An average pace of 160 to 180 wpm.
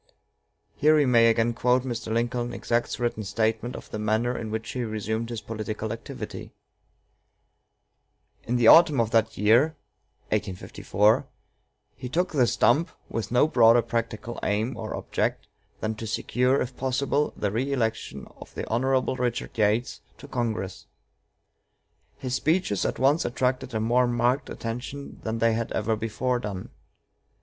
No: average, 140 wpm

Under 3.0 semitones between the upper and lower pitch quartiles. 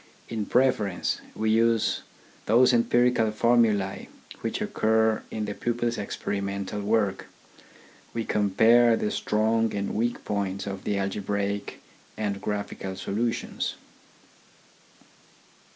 Yes: narrow, 2.4 semitones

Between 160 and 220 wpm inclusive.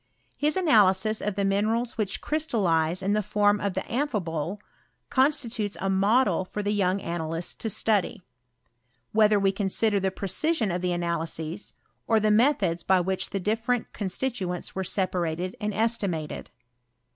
No: average, 150 wpm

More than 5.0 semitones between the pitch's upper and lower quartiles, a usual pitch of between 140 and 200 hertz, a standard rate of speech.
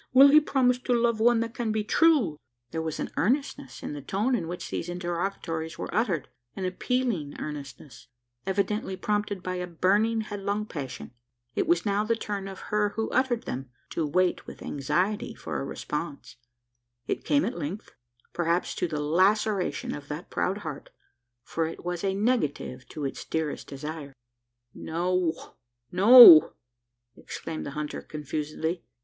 Yes: wide, 5.5 semitones; medium, 185 Hz; average, 160 wpm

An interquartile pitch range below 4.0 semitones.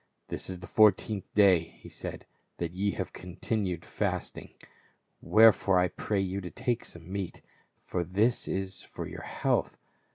Yes: narrow, 2.4 semitones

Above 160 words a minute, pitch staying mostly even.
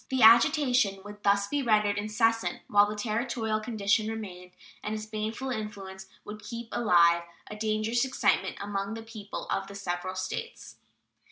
No: average, 155 wpm; narrow, 2.1 semitones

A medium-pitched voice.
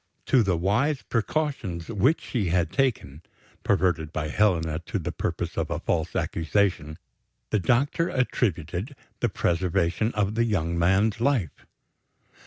No: very low, 95 Hz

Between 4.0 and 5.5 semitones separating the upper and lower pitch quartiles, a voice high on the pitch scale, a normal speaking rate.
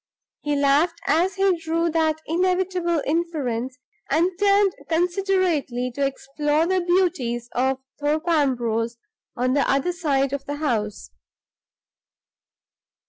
No: average, 4.5 semitones; very high, 310 Hz; slow, 115 wpm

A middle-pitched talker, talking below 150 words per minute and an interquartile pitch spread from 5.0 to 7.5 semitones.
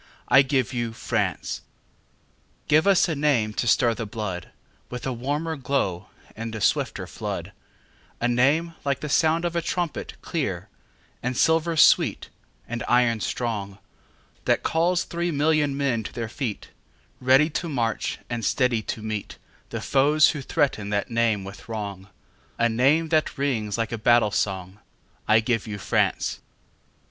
No: low, 125 Hz; slow, 135 wpm; wide, 5.4 semitones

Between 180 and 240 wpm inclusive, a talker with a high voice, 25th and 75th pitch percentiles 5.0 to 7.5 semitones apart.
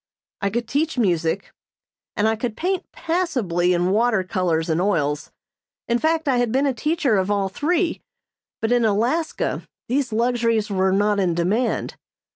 No: average, 160 wpm; high, 220 Hz; wide, 5.4 semitones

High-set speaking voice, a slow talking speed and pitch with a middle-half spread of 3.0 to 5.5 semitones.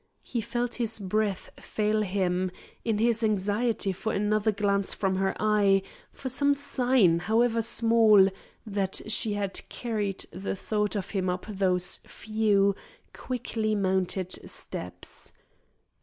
No: high, 210 Hz; slow, 125 wpm; narrow, 2.6 semitones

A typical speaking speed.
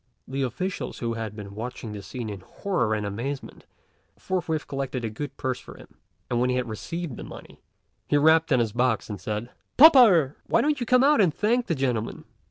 No: fast, 210 wpm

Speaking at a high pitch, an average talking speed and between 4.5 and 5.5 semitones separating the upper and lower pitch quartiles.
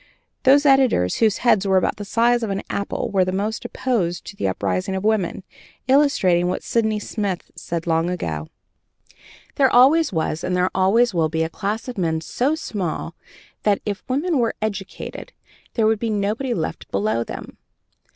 Yes: high, 200 Hz; average, 175 wpm; average, 4.9 semitones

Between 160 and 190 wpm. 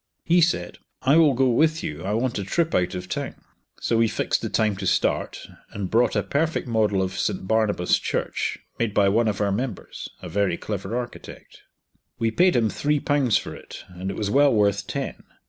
No: fast, 205 wpm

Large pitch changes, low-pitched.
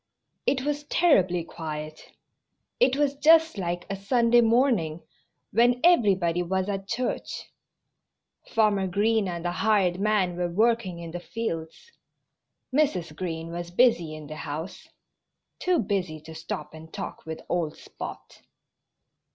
No: wide, 5.7 semitones; high, 190 Hz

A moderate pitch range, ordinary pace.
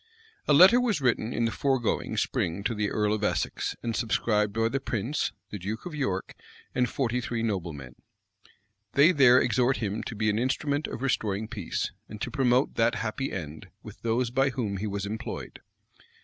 Yes: average, 3.9 semitones; average, 185 wpm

